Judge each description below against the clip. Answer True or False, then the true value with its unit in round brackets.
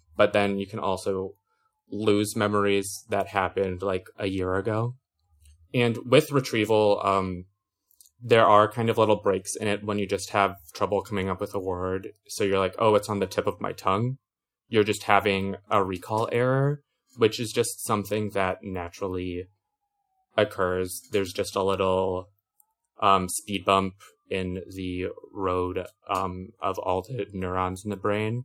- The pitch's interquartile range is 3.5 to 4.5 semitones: False (2.6 semitones)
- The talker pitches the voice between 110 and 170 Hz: False (100 Hz)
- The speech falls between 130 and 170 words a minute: True (160 wpm)